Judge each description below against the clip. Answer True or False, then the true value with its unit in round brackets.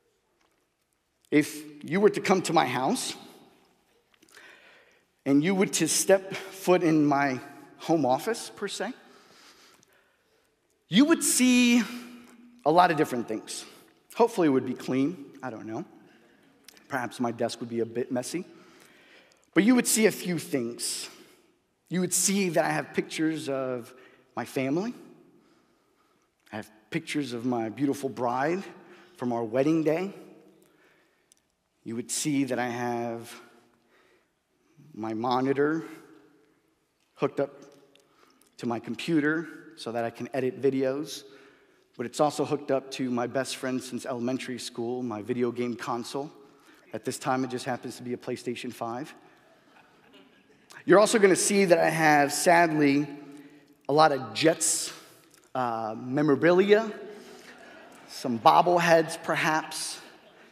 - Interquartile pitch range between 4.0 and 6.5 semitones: True (5.6 semitones)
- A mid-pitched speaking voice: True (145 Hz)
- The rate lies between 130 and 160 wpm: True (135 wpm)